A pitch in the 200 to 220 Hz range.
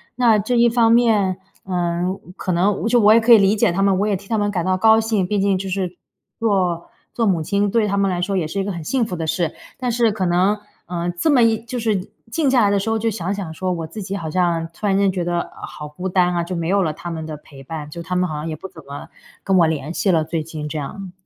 No: high, 190 Hz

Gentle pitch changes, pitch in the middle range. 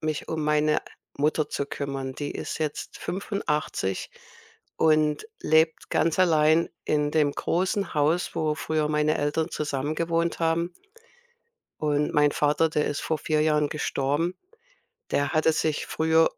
Yes: narrow, 1.5 semitones; medium, 155 Hz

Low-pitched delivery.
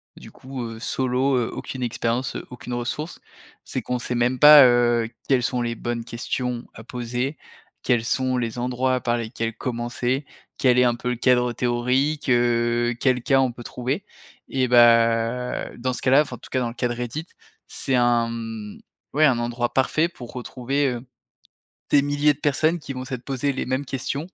Yes: low, 125 Hz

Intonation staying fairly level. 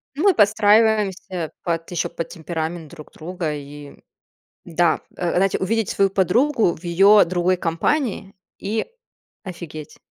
No: average, 3.8 semitones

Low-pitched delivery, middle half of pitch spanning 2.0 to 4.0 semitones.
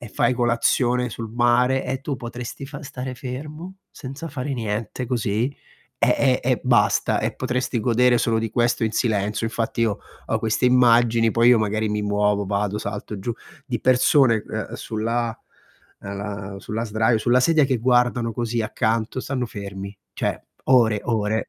Yes: low, 120 Hz; average, 2.7 semitones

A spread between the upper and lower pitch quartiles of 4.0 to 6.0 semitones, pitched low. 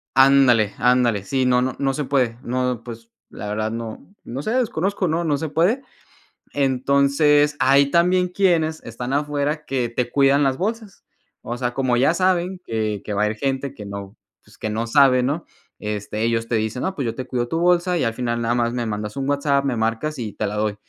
Yes: average, 4.4 semitones; low, 130 Hz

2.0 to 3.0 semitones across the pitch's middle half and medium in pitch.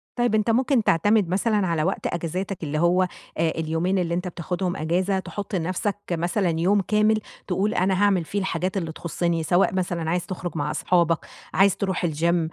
Yes: average, 2.7 semitones; medium, 180 Hz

